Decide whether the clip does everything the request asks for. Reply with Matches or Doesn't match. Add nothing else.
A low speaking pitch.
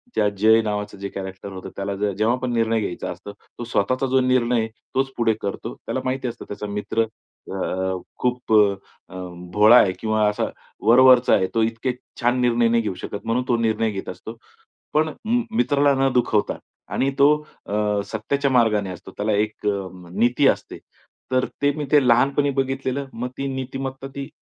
Matches